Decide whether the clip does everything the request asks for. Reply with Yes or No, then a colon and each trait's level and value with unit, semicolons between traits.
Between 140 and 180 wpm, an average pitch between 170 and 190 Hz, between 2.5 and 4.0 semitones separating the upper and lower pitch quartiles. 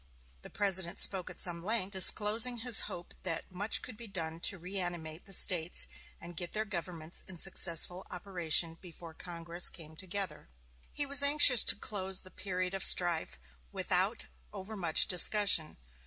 Yes: average, 155 wpm; medium, 185 Hz; average, 3.1 semitones